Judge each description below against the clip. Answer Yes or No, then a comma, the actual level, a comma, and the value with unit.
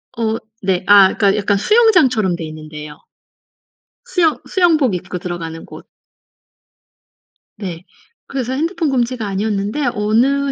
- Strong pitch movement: Yes, wide, 6.9 semitones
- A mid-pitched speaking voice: No, high, 215 Hz